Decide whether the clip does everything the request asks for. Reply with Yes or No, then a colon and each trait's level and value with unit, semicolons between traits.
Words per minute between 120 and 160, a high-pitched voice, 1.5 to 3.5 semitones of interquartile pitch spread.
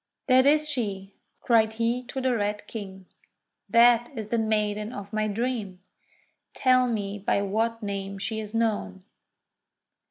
Yes: average, 145 wpm; high, 220 Hz; average, 2.7 semitones